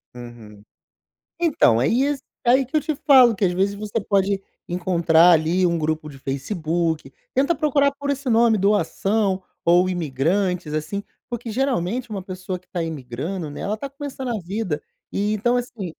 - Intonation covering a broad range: Yes, wide, 6.4 semitones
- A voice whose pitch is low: No, high, 195 Hz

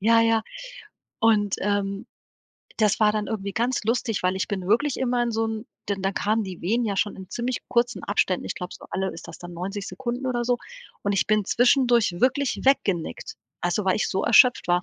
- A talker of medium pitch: No, high, 215 Hz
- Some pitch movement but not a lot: Yes, average, 3.6 semitones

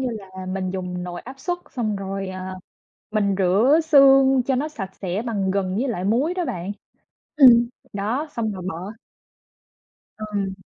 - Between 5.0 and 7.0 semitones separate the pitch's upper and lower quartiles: Yes, wide, 5.5 semitones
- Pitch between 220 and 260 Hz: No, high, 205 Hz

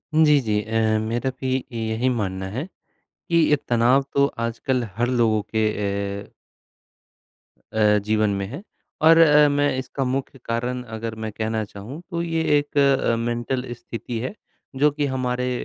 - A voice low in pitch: Yes, low, 120 Hz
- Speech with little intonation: No, average, 3.9 semitones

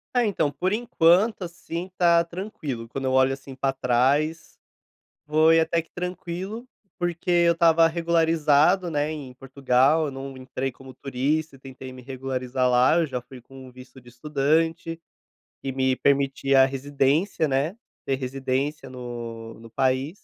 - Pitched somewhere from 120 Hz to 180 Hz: Yes, medium, 140 Hz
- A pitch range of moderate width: Yes, average, 4.1 semitones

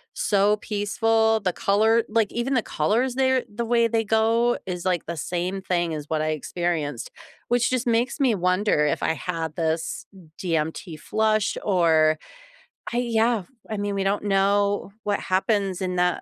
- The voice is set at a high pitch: Yes, high, 200 Hz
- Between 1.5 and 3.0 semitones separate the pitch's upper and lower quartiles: No, average, 4.3 semitones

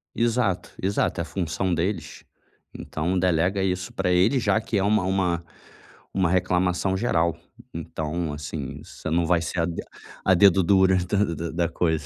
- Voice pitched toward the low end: Yes, very low, 90 Hz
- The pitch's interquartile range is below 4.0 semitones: Yes, narrow, 2.4 semitones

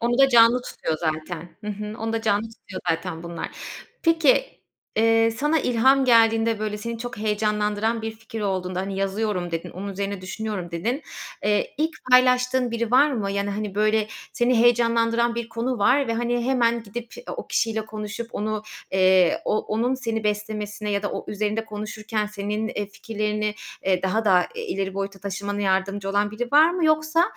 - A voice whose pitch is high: Yes, high, 215 Hz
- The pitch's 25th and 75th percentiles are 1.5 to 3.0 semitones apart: Yes, average, 2.7 semitones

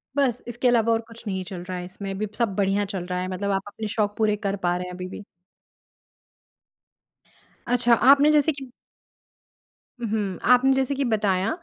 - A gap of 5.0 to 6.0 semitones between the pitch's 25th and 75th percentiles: No, average, 4.3 semitones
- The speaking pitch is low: No, high, 210 Hz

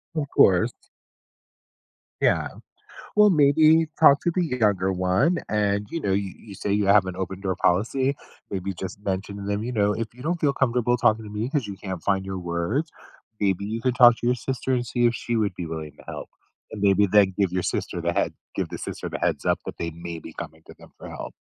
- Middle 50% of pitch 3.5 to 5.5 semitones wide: Yes, average, 4.7 semitones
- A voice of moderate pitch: No, low, 105 Hz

